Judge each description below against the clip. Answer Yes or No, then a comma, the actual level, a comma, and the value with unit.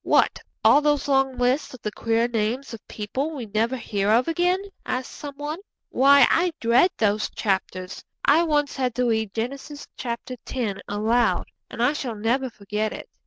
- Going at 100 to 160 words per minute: No, average, 170 wpm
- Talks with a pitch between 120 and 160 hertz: No, high, 245 Hz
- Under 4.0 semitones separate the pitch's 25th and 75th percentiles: No, average, 4.3 semitones